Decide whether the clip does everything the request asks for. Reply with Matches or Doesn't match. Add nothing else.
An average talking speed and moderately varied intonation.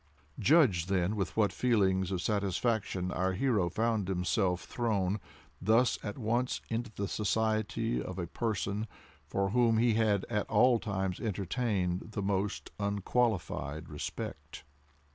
Doesn't match